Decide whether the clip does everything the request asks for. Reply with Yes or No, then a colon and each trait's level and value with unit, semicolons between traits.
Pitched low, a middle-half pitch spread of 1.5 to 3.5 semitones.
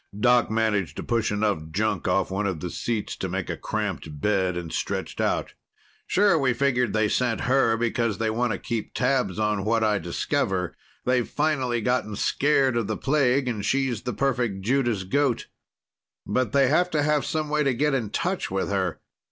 No: low, 115 Hz; average, 4.8 semitones